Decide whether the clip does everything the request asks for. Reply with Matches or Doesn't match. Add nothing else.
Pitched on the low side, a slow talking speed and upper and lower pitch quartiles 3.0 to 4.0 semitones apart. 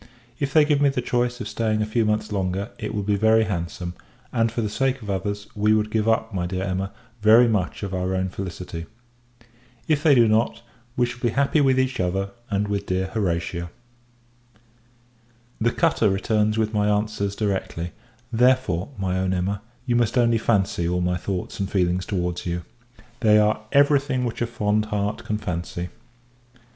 Doesn't match